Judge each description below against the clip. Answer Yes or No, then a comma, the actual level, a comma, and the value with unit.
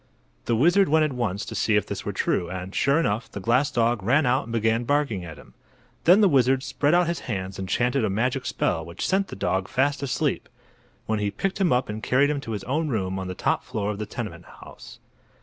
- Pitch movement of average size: No, wide, 5.9 semitones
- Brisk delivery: Yes, fast, 240 wpm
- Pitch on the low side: Yes, low, 120 Hz